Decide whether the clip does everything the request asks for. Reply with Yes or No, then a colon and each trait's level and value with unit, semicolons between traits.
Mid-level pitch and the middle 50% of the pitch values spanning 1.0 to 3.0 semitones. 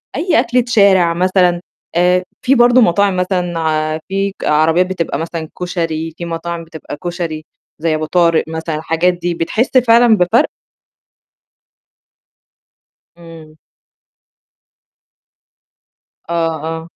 Yes: medium, 175 Hz; average, 2.7 semitones